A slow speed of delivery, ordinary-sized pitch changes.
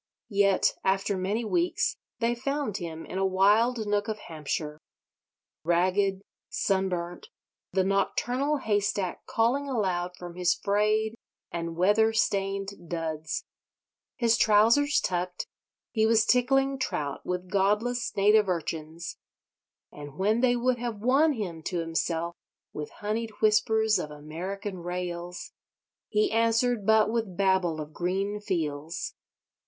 Yes: slow, 125 wpm; average, 4.1 semitones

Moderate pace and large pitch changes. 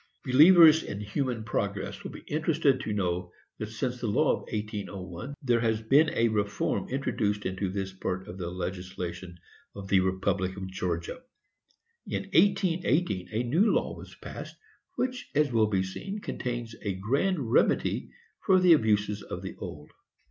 Yes: average, 160 wpm; wide, 6.6 semitones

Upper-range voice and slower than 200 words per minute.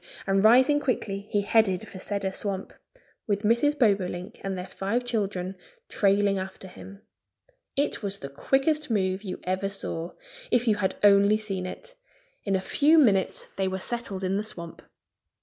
Yes: high, 200 Hz; average, 165 wpm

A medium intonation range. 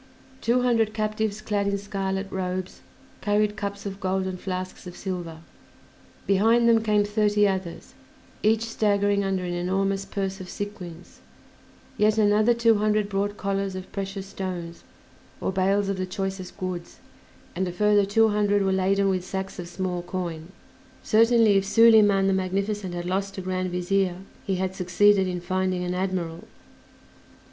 No: narrow, 1.9 semitones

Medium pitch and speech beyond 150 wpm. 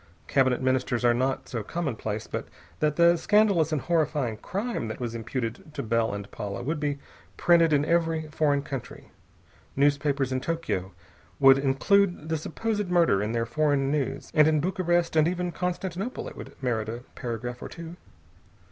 Yes: medium, 145 Hz; average, 165 wpm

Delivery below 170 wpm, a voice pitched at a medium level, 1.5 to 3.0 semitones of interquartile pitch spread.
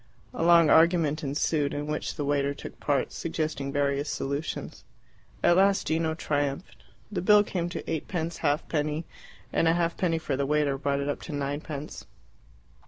Yes: average, 160 wpm; medium, 150 Hz; average, 2.7 semitones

